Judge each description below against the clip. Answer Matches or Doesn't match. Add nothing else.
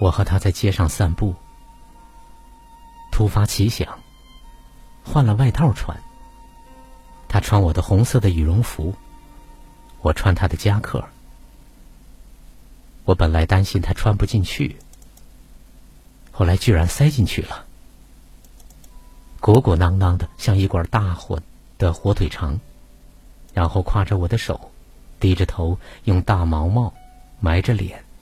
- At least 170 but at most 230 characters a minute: Matches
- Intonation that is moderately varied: Matches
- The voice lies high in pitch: Doesn't match